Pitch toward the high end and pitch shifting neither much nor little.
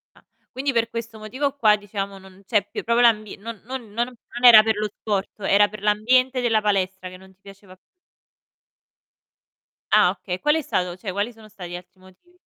Yes: high, 215 Hz; average, 3.3 semitones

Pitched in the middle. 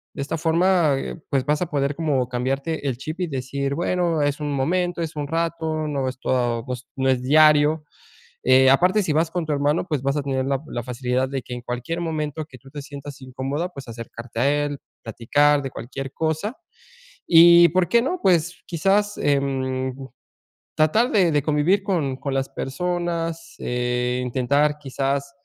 Yes: medium, 145 Hz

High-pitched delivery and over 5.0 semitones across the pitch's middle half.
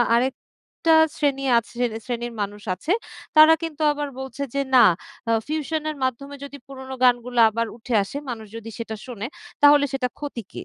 No: very high, 260 Hz; average, 3.6 semitones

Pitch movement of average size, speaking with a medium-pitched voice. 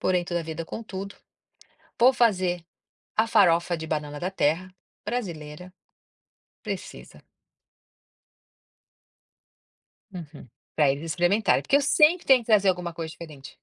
Yes: average, 4.4 semitones; medium, 175 Hz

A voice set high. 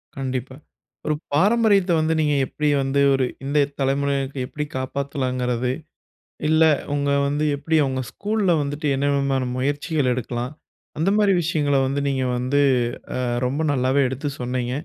No: medium, 140 Hz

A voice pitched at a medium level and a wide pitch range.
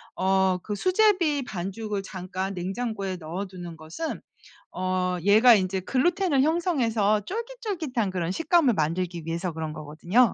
No: high, 195 Hz; wide, 6.9 semitones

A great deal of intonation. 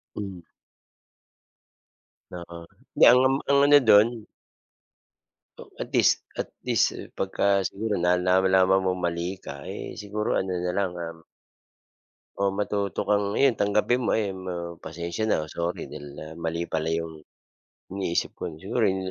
No: average, 3.2 semitones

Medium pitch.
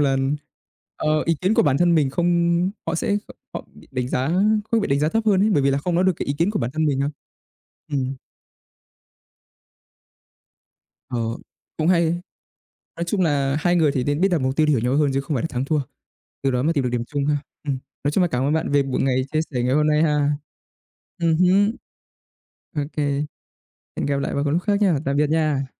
Yes: medium, 150 Hz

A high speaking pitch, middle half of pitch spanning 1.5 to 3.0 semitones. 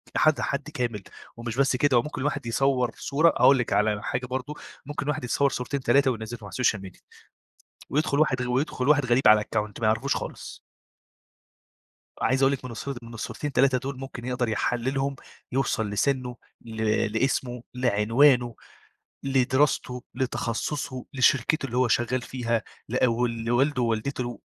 No: low, 125 Hz; average, 2.7 semitones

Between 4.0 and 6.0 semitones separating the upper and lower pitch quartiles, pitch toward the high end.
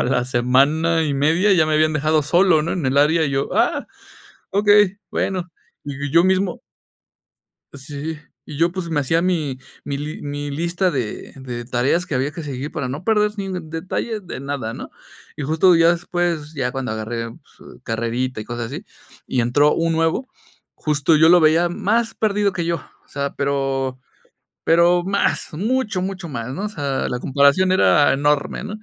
No: average, 4.4 semitones; medium, 155 Hz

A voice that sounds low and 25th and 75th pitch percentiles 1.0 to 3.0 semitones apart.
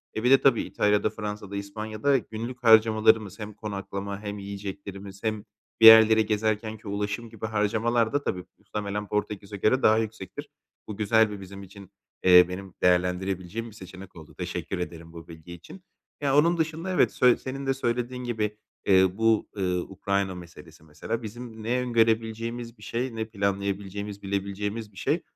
Yes: low, 105 Hz; narrow, 2.5 semitones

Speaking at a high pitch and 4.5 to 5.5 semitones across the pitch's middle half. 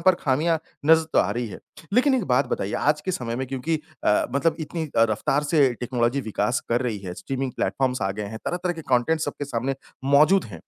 No: low, 135 Hz; average, 5.2 semitones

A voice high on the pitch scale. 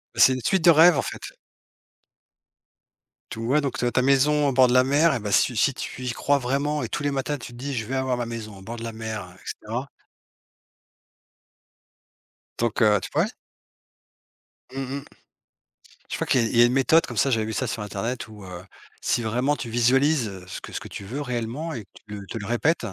No: low, 125 Hz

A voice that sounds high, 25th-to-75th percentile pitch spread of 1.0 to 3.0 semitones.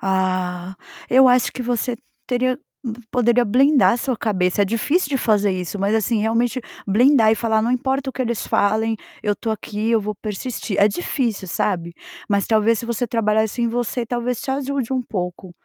No: high, 225 Hz; average, 3.5 semitones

